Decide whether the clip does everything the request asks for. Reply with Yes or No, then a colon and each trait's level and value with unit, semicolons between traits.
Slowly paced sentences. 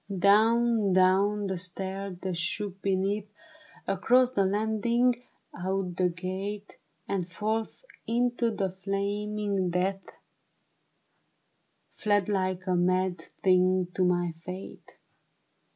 Yes: slow, 105 wpm